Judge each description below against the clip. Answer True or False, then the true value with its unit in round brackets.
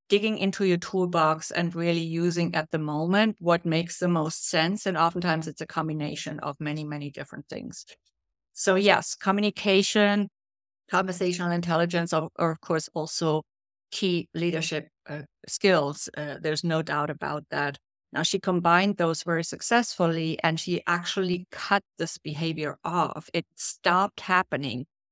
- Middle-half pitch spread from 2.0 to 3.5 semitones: True (2.9 semitones)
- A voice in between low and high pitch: True (165 Hz)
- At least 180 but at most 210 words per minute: False (145 wpm)